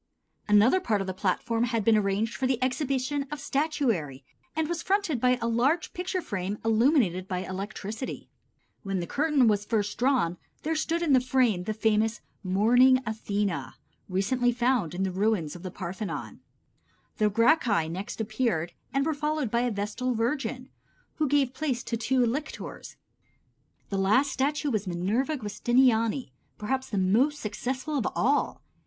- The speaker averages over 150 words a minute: Yes, average, 160 wpm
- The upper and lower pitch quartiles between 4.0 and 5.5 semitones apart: Yes, average, 4.9 semitones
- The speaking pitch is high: Yes, high, 230 Hz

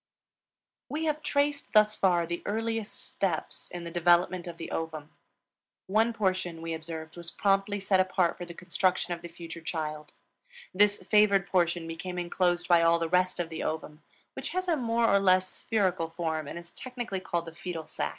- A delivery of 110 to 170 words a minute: No, average, 185 wpm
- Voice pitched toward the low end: No, medium, 180 Hz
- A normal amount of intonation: Yes, average, 3.1 semitones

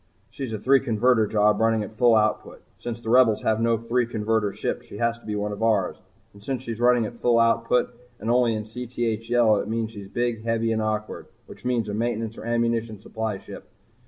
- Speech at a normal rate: No, fast, 220 wpm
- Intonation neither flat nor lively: No, narrow, 1.6 semitones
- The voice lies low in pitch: Yes, low, 115 Hz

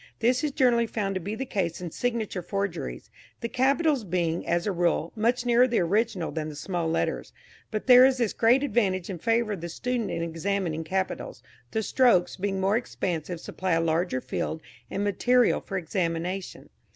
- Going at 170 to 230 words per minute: Yes, average, 185 wpm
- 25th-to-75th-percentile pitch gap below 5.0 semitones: No, wide, 5.6 semitones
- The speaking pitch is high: Yes, high, 195 Hz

